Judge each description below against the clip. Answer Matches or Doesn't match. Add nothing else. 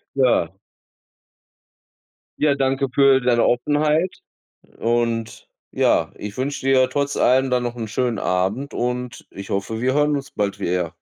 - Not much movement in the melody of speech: Doesn't match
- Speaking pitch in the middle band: Doesn't match